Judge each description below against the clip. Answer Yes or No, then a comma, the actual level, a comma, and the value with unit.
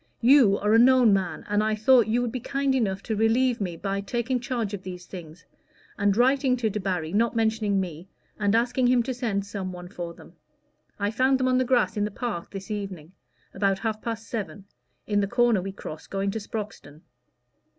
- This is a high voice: Yes, high, 210 Hz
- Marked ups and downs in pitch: No, average, 3.7 semitones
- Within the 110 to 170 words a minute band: No, fast, 205 wpm